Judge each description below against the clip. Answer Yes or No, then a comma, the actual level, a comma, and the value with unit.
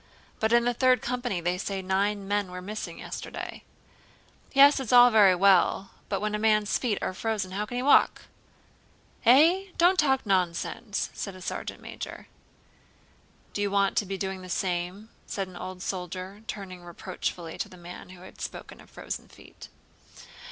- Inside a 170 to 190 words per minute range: Yes, average, 175 wpm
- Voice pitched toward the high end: Yes, high, 200 Hz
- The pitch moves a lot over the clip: No, average, 3.5 semitones